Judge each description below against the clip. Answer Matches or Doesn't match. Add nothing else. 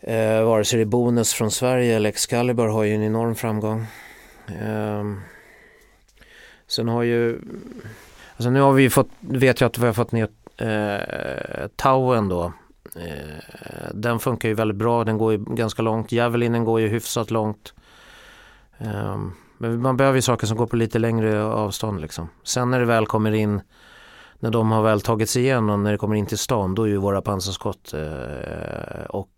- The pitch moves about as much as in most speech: Doesn't match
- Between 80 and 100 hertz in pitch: Doesn't match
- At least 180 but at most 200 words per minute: Matches